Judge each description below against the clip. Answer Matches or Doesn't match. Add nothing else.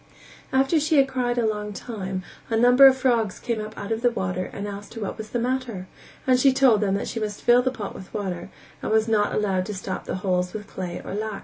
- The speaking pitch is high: Matches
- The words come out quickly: Matches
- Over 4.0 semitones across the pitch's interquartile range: Doesn't match